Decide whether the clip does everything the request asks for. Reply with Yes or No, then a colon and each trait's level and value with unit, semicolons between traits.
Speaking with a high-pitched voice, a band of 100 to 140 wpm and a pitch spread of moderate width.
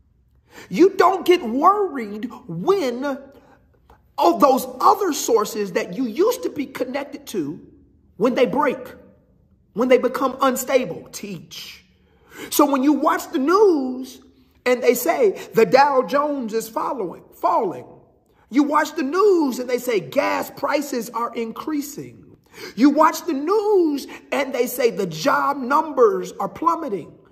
Yes: very high, 280 Hz; slow, 135 wpm; average, 4.9 semitones